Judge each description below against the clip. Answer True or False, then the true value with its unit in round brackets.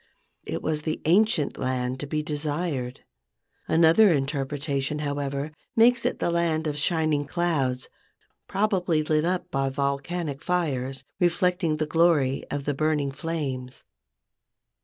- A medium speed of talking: False (125 wpm)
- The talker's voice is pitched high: False (150 Hz)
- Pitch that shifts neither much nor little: True (3.5 semitones)